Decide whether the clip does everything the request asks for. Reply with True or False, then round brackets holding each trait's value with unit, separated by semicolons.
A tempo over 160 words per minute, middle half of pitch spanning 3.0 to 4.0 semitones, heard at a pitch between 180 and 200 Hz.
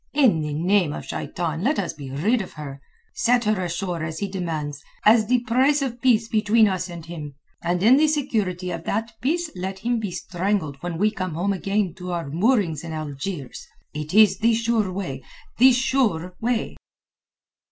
False (180 wpm; 5.5 semitones; 190 Hz)